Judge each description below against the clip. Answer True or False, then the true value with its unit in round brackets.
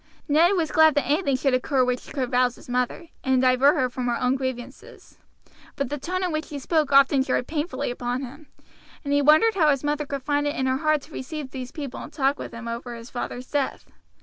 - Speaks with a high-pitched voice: True (275 Hz)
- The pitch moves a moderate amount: True (3.0 semitones)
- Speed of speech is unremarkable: False (230 wpm)